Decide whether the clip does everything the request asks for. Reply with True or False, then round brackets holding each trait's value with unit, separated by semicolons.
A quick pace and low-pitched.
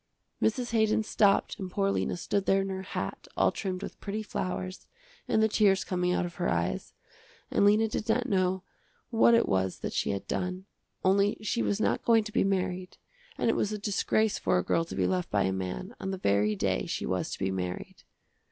False (215 wpm; 190 Hz)